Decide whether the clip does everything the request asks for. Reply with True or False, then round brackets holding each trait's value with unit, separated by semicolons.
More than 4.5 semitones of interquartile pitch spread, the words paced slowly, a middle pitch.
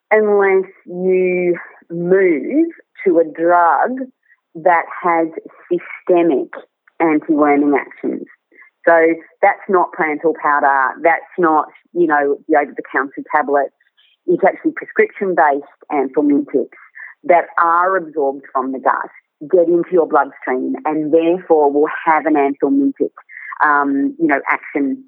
True (5.0 semitones; 115 wpm; 170 Hz)